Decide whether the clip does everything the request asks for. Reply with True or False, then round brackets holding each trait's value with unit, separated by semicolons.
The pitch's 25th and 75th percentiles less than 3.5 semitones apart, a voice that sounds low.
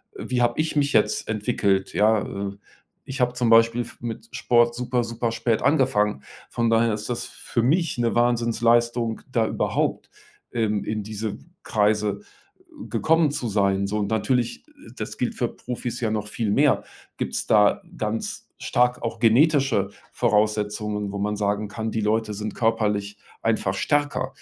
True (2.6 semitones; 115 Hz)